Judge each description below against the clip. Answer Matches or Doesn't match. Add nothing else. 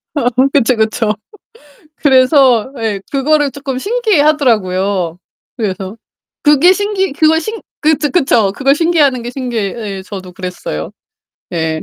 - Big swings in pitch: Matches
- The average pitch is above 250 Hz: Matches